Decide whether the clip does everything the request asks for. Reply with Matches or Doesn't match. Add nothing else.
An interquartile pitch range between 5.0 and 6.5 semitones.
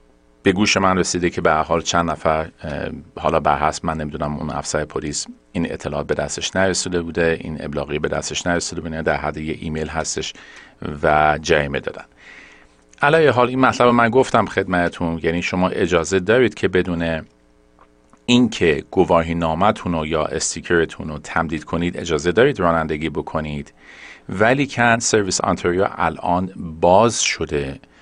Doesn't match